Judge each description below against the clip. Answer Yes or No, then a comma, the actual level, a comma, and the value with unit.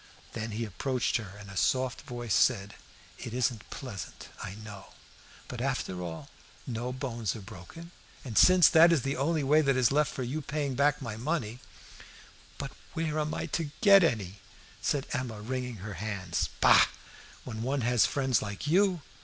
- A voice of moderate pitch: No, low, 125 Hz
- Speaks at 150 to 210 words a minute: Yes, average, 180 wpm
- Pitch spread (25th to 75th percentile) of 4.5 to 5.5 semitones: Yes, average, 5.1 semitones